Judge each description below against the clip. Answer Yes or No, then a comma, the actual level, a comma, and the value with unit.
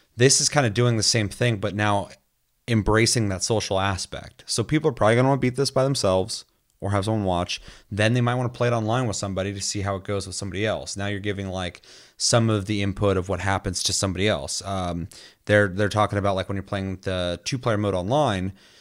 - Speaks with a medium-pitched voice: No, low, 100 Hz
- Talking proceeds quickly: Yes, fast, 245 wpm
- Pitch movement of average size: Yes, average, 3.1 semitones